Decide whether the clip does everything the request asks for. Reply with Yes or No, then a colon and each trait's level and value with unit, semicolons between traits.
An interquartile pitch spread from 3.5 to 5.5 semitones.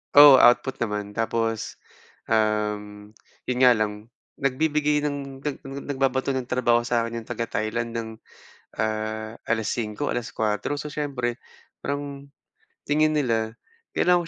Yes: average, 4.3 semitones